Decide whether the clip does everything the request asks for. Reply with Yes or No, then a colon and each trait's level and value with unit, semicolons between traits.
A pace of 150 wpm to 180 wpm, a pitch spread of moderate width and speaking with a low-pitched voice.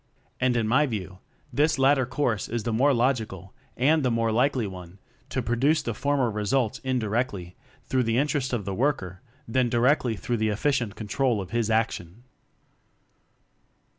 Yes: average, 165 wpm; average, 3.7 semitones; low, 120 Hz